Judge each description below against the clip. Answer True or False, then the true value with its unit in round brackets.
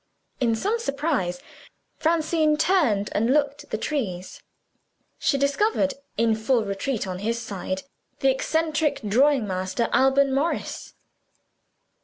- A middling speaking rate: False (120 wpm)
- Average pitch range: False (5.9 semitones)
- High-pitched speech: True (270 Hz)